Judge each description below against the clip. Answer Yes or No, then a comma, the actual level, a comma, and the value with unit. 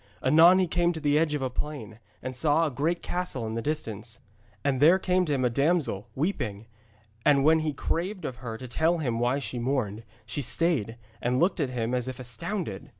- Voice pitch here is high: No, medium, 140 Hz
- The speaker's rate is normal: No, fast, 210 wpm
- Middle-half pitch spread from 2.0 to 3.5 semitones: No, average, 5.1 semitones